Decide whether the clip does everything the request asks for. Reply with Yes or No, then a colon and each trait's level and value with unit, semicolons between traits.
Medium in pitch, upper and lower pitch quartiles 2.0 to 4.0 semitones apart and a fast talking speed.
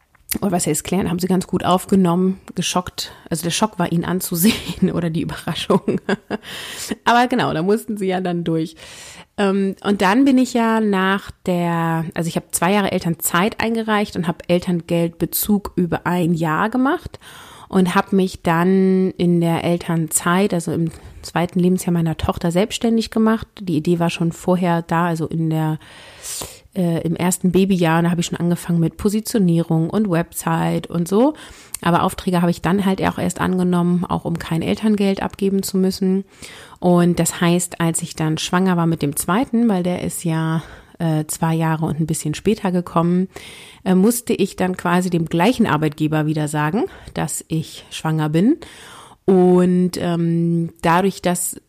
No: medium, 175 Hz; average, 2.7 semitones; average, 165 wpm